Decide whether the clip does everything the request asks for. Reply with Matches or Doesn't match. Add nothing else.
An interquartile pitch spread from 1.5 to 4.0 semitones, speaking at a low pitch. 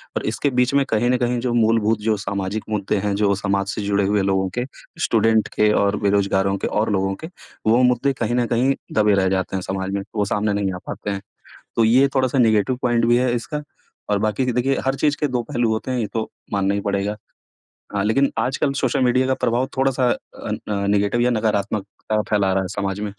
Matches